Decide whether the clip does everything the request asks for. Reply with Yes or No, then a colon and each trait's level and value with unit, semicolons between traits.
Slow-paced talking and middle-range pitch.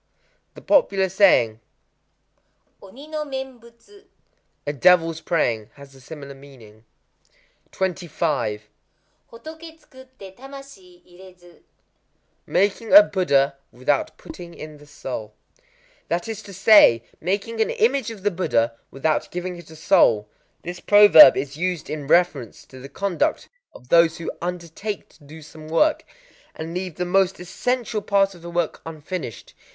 Yes: slow, 130 wpm; medium, 175 Hz